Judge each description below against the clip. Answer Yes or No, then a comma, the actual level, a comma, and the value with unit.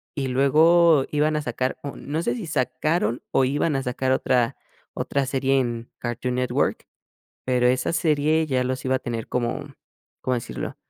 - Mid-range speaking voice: No, low, 130 Hz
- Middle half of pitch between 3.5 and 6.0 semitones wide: No, average, 3.1 semitones